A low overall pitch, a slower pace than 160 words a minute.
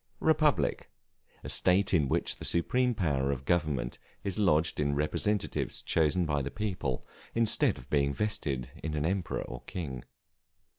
Yes: very low, 80 Hz; average, 150 wpm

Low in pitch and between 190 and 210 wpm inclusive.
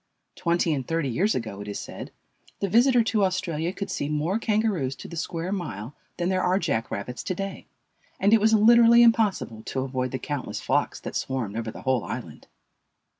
No: medium, 170 Hz; average, 195 wpm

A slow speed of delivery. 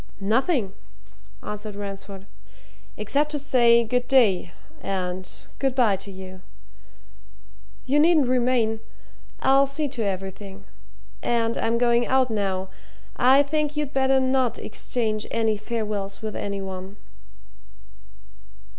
Yes: slow, 115 wpm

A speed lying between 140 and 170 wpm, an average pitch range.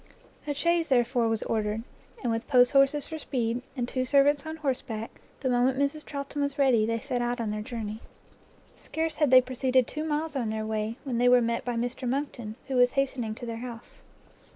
No: average, 200 wpm; average, 3.3 semitones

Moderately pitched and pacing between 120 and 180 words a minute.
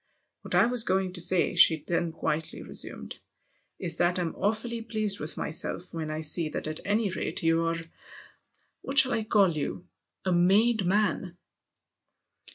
Yes: medium, 180 Hz; average, 165 wpm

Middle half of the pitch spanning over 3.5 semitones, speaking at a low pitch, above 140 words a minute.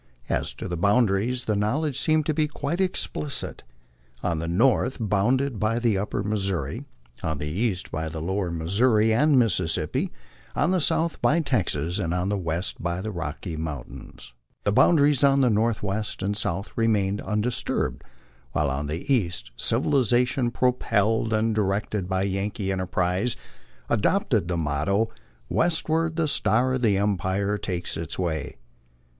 Yes: wide, 5.6 semitones; low, 105 Hz; average, 150 wpm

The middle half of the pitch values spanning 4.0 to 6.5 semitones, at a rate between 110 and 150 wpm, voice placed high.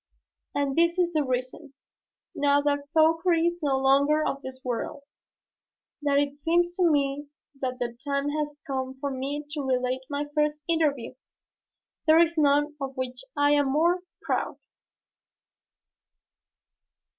No: narrow, 2.5 semitones; average, 140 wpm; very high, 285 Hz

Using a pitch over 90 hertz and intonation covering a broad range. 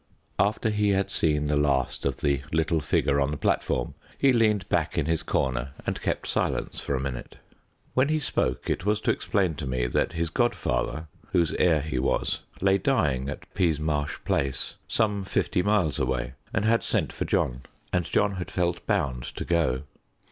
No: very low, 80 Hz; wide, 6.3 semitones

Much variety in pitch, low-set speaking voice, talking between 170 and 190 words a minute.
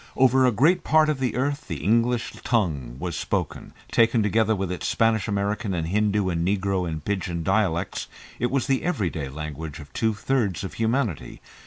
Yes: wide, 5.7 semitones; low, 105 Hz; average, 180 wpm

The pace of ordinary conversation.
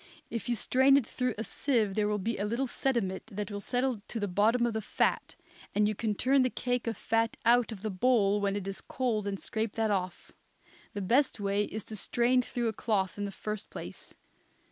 No: fast, 225 wpm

